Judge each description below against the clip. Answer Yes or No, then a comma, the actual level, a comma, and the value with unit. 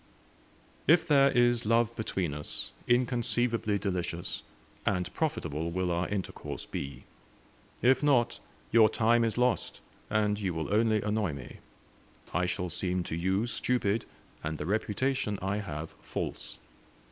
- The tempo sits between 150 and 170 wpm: No, slow, 135 wpm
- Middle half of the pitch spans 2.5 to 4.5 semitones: No, average, 4.9 semitones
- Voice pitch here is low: Yes, low, 105 Hz